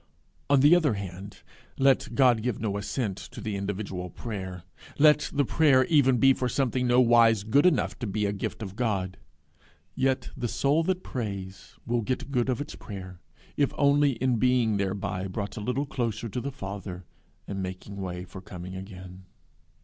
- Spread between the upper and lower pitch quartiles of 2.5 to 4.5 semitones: No, average, 5.2 semitones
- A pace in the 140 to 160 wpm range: No, average, 175 wpm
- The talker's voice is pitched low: Yes, low, 115 Hz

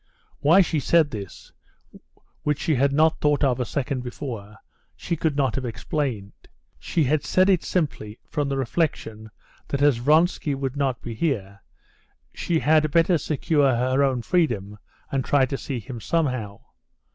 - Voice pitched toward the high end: No, medium, 140 Hz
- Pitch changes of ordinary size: Yes, average, 4.2 semitones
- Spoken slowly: No, average, 160 wpm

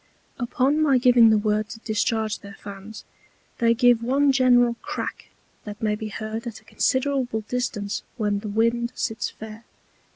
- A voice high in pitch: Yes, high, 225 Hz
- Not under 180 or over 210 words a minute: No, average, 160 wpm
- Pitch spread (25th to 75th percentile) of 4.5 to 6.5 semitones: No, narrow, 2.5 semitones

